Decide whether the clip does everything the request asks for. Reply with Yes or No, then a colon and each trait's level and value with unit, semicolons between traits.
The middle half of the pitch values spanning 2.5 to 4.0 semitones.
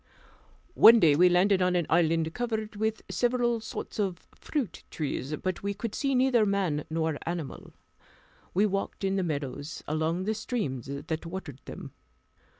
No: average, 5.3 semitones